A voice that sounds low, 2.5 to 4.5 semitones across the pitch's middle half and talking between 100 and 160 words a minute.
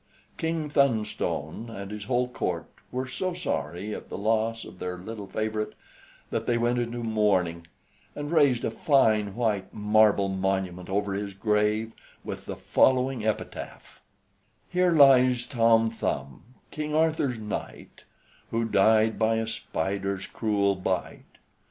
Yes: low, 110 Hz; average, 3.8 semitones; slow, 135 wpm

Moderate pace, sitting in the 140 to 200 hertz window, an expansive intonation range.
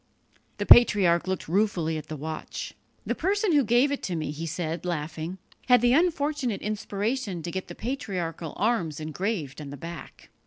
Yes: average, 165 wpm; medium, 185 Hz; wide, 7.0 semitones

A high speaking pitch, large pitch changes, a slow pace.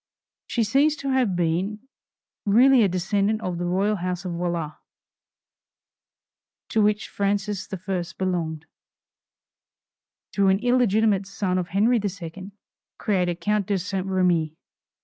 No: high, 195 Hz; average, 2.9 semitones; slow, 125 wpm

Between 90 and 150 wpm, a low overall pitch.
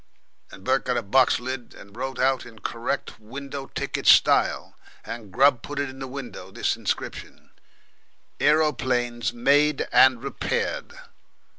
Yes: slow, 135 wpm; low, 130 Hz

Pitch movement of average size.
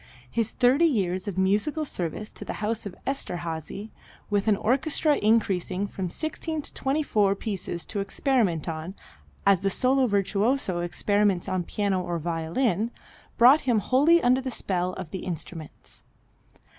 No: wide, 5.8 semitones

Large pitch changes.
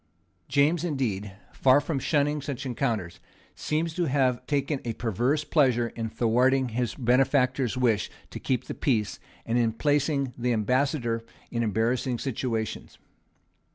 No: average, 3.4 semitones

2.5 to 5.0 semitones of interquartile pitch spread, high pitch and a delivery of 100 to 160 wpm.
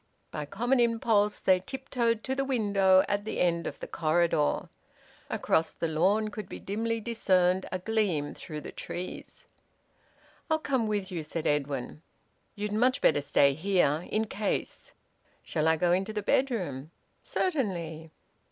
No: wide, 5.5 semitones; high, 195 Hz; average, 150 wpm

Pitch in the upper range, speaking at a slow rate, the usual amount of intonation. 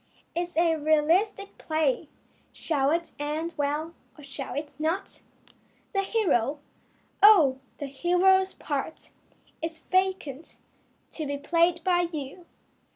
Yes: very high, 320 Hz; slow, 120 wpm; average, 3.3 semitones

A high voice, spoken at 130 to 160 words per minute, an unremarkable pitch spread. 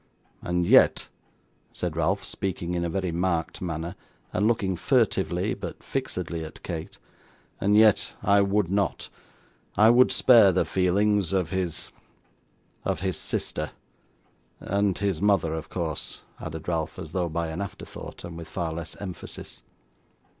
No: very low, 90 Hz; average, 145 wpm; average, 3.1 semitones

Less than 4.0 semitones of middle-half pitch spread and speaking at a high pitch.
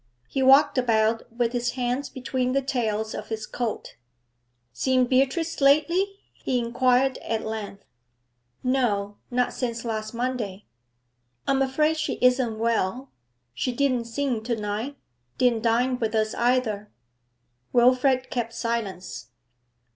Yes: average, 2.8 semitones; high, 245 Hz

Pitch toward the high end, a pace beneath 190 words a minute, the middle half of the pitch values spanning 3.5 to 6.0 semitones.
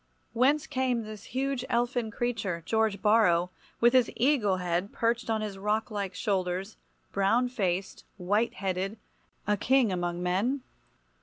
Yes: high, 215 Hz; slow, 135 wpm; average, 4.1 semitones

